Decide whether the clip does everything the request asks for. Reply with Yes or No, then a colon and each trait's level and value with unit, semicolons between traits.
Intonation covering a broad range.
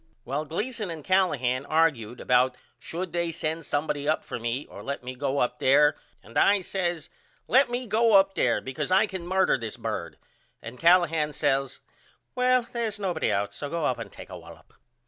Yes: wide, 6.1 semitones